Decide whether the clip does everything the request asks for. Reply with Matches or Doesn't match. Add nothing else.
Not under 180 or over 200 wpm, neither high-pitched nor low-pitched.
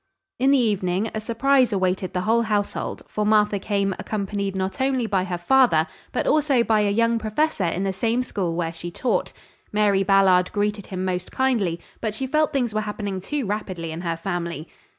Doesn't match